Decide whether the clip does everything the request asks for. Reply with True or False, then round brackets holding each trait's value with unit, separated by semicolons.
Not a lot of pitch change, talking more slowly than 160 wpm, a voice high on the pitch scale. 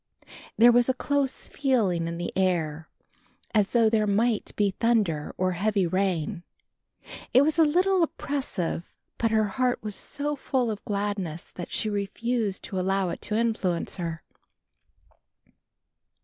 False (4.8 semitones; 145 wpm; 210 Hz)